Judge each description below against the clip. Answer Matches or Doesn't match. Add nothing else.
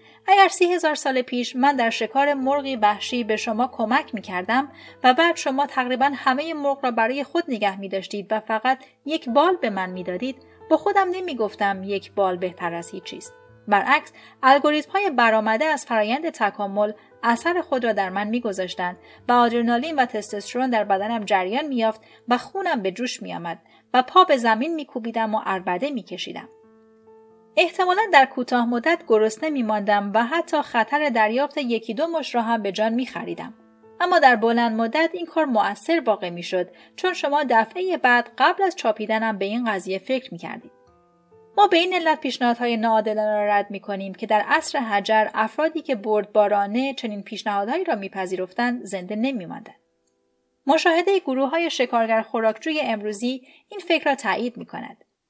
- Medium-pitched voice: Doesn't match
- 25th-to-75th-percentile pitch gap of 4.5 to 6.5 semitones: Matches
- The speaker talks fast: Matches